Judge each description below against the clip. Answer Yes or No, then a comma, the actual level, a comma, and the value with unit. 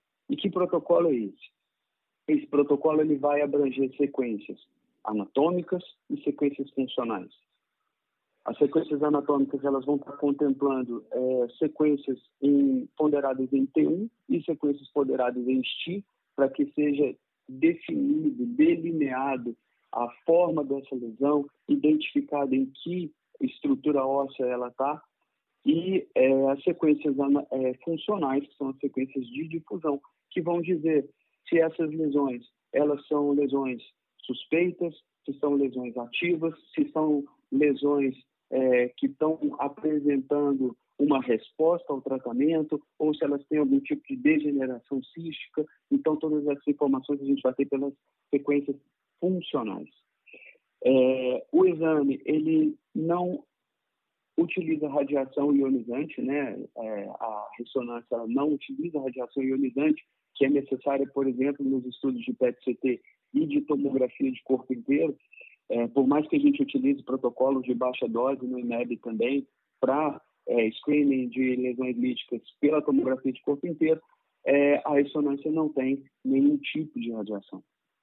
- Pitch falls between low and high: Yes, medium, 145 Hz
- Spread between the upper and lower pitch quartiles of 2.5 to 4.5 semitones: Yes, average, 3.8 semitones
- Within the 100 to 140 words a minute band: Yes, average, 130 wpm